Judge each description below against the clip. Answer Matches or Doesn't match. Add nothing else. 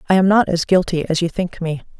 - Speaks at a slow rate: Doesn't match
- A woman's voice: Matches